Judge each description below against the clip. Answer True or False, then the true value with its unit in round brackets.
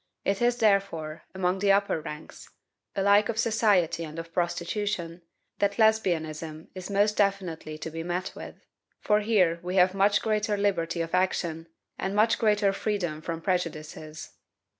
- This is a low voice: False (185 Hz)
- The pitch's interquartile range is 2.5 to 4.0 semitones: True (3.6 semitones)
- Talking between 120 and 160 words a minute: True (150 wpm)